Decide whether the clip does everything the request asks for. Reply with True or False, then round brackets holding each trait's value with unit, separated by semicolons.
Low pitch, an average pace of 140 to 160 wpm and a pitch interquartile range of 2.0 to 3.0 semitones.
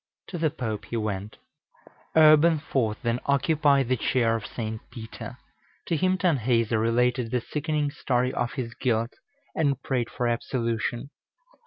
False (125 Hz; 145 wpm; 3.8 semitones)